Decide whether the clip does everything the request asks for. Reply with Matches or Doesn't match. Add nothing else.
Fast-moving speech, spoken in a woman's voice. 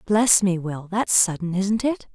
Doesn't match